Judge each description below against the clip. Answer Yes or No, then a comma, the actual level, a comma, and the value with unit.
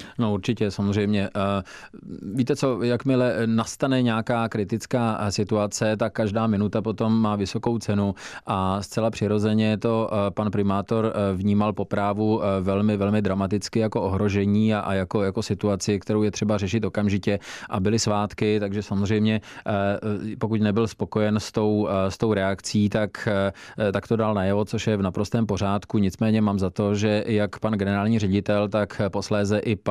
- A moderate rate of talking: Yes, average, 150 wpm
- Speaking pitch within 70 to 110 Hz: Yes, low, 105 Hz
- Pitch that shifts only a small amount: Yes, narrow, 1.7 semitones